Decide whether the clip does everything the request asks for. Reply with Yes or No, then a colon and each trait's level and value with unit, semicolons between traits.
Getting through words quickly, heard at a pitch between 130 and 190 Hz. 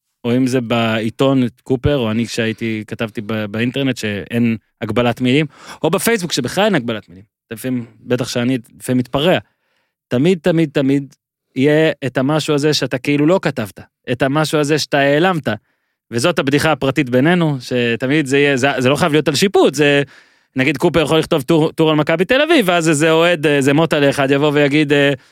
Yes: fast, 175 wpm; medium, 140 Hz